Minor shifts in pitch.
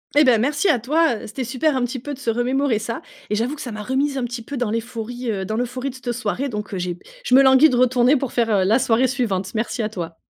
No: average, 3.1 semitones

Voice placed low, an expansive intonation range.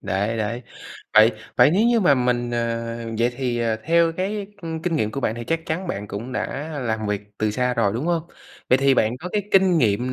Yes: low, 125 Hz; wide, 6.4 semitones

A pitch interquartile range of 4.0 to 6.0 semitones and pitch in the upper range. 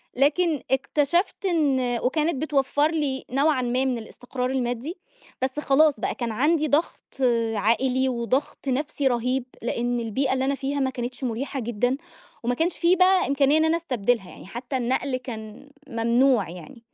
No: average, 3.2 semitones; very high, 265 Hz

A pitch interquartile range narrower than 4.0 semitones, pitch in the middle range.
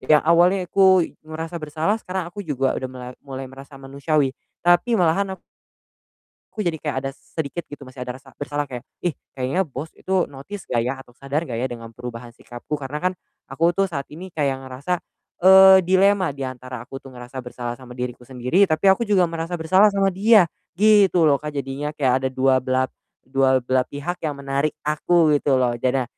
No: average, 5.2 semitones; medium, 145 Hz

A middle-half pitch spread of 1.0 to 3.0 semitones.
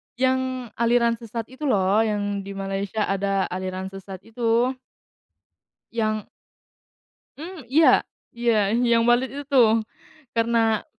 No: average, 3.5 semitones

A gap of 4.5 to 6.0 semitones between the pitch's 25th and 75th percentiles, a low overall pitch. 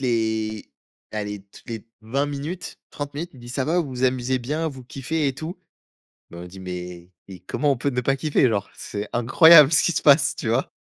Yes: average, 5.0 semitones; low, 130 Hz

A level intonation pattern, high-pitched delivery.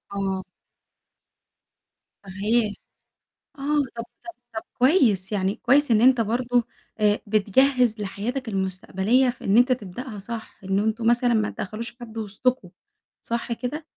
No: average, 3.6 semitones; high, 230 Hz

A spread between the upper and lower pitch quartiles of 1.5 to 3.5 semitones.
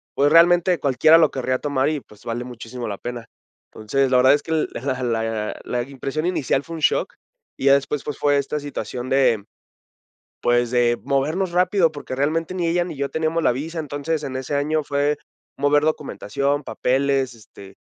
No: average, 3.9 semitones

